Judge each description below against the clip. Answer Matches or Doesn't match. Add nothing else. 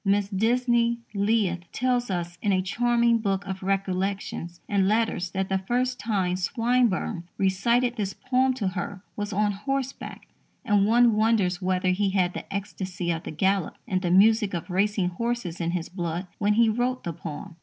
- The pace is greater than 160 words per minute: Matches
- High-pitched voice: Matches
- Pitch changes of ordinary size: Matches